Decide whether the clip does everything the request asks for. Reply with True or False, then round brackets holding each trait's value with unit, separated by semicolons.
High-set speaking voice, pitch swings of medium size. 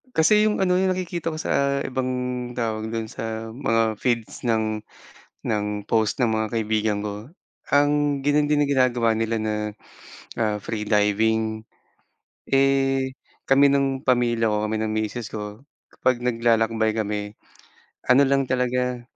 False (115 Hz; 3.7 semitones)